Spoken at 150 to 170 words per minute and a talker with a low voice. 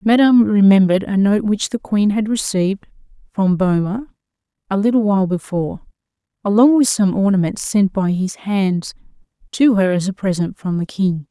No: average, 165 wpm; high, 200 Hz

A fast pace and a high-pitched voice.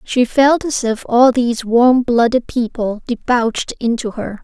No: average, 160 wpm; high, 240 Hz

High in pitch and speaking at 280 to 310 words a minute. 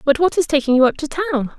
Yes: very high, 295 Hz; fast, 305 wpm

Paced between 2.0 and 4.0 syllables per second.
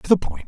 No: 7.0 syllables/s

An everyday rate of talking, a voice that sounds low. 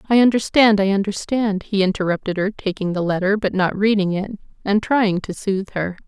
No: average, 190 wpm; high, 200 Hz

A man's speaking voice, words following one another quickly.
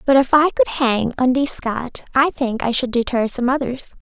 No: female; fast, 210 wpm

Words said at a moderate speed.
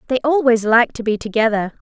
Yes: average, 190 wpm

